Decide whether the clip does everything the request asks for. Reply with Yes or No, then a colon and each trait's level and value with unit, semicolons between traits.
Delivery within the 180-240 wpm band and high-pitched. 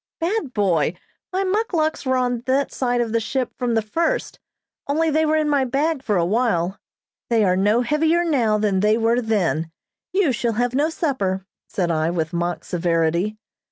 Yes: average, 185 wpm; high, 235 Hz